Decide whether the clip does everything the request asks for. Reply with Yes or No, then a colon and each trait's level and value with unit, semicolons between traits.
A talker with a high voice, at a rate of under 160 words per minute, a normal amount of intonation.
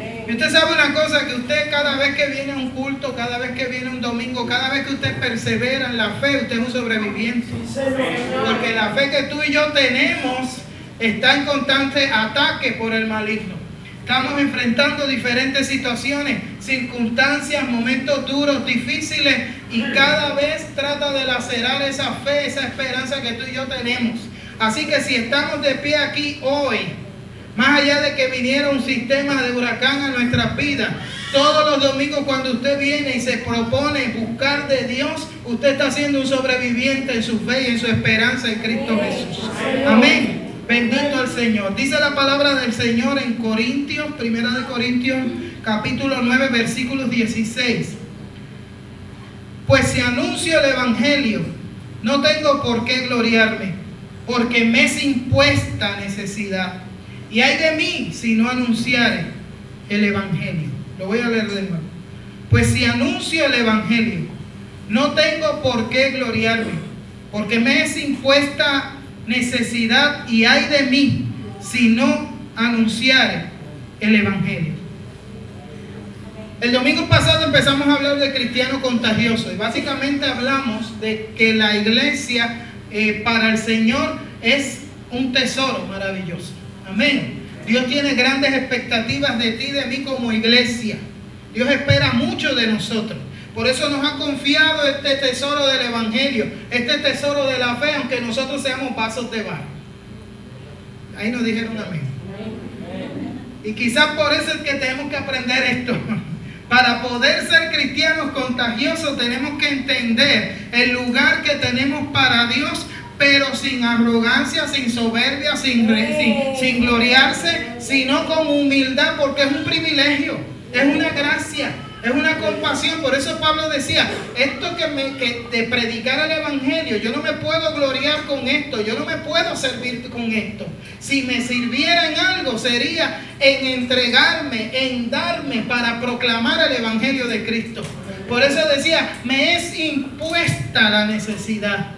Yes: very high, 260 Hz; average, 145 wpm; average, 3.5 semitones